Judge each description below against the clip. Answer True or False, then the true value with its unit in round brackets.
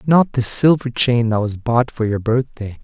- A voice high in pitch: False (125 Hz)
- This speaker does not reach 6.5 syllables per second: True (4.5 syllables/s)